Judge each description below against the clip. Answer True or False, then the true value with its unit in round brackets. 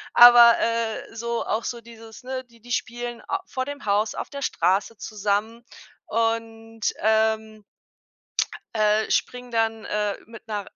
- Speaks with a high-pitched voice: True (225 Hz)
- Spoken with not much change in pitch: True (1.5 semitones)